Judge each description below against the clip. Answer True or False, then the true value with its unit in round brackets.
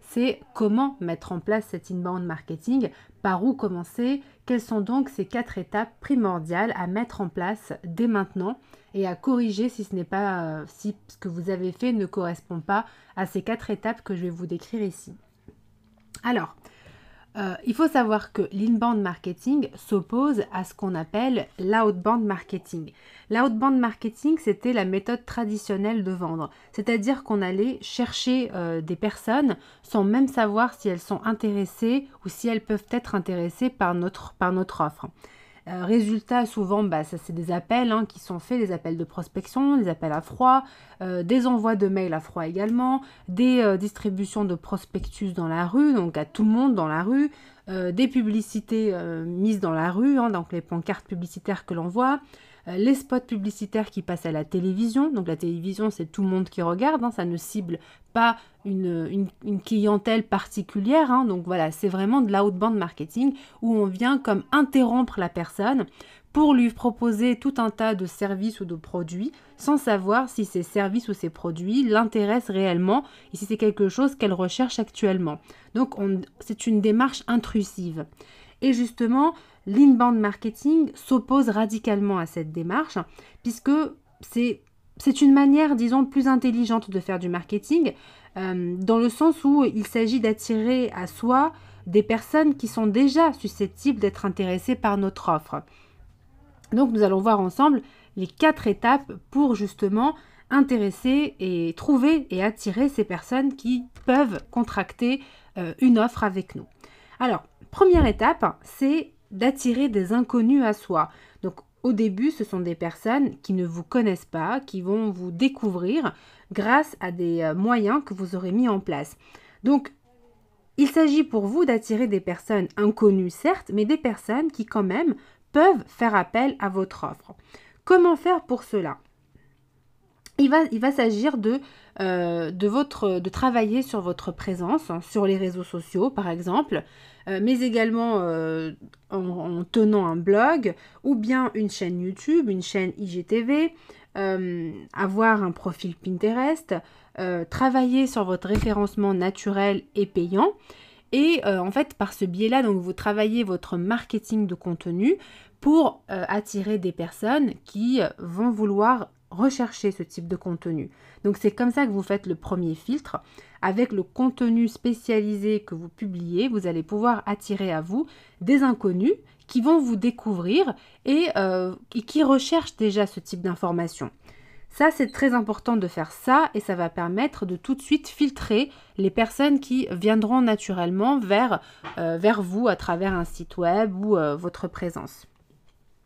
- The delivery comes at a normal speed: True (165 wpm)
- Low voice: False (210 Hz)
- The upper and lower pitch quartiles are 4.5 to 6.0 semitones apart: True (5.0 semitones)